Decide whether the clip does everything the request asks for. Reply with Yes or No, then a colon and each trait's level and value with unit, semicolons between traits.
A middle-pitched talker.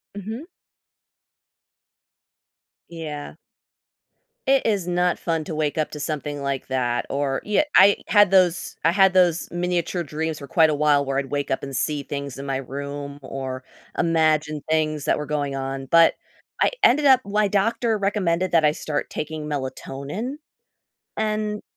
Yes: medium, 155 Hz